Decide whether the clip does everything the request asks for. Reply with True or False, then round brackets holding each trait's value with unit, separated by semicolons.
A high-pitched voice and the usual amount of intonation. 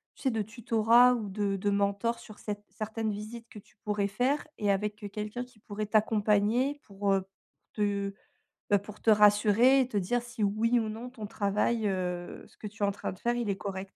False (210 Hz; 2.3 semitones)